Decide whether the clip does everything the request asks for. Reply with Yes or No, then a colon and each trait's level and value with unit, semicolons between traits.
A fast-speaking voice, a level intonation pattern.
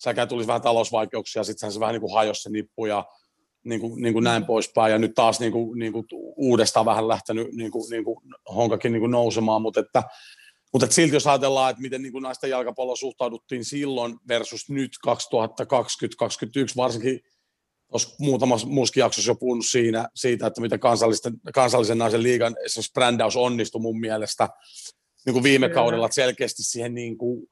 Yes: fast, 175 wpm; narrow, 2.0 semitones